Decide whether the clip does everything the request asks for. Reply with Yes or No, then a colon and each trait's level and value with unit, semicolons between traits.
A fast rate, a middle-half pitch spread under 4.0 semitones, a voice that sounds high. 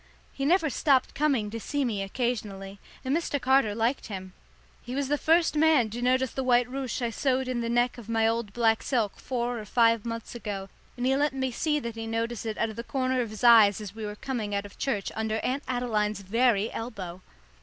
Yes: fast, 225 wpm; average, 3.2 semitones; high, 235 Hz